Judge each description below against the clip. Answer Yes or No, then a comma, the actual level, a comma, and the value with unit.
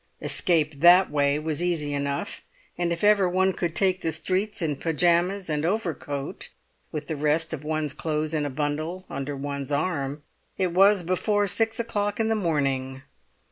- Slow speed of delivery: No, average, 170 wpm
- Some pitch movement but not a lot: Yes, average, 4.2 semitones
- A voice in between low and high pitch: Yes, medium, 160 Hz